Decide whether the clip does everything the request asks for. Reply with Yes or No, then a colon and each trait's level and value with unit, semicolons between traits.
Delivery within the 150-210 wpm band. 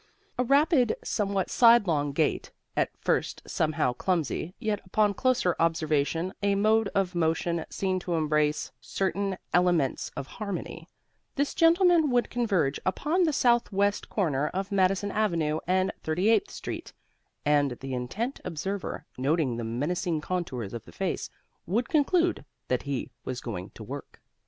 No: average, 140 wpm